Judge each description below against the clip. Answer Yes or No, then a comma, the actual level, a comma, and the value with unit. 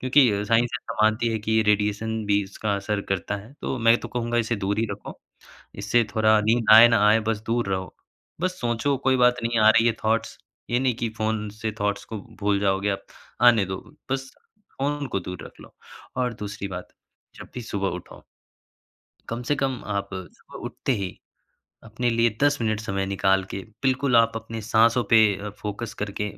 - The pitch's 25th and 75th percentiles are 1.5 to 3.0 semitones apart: Yes, average, 2.7 semitones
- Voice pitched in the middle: No, low, 110 Hz